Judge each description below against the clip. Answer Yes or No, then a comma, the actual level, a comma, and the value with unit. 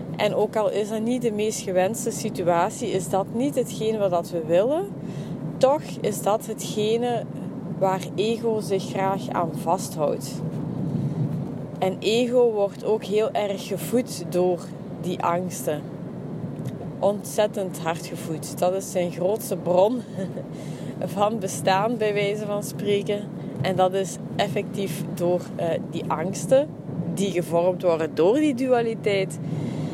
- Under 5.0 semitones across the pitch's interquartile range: Yes, average, 3.4 semitones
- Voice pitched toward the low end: No, high, 190 Hz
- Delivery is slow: Yes, slow, 130 wpm